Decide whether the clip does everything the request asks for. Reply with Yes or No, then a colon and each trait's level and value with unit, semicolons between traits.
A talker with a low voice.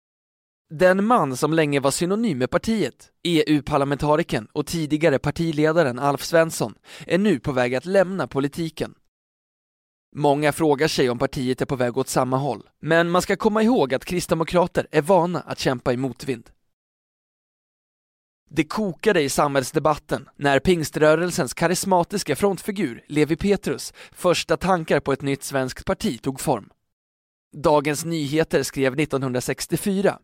No: medium, 155 Hz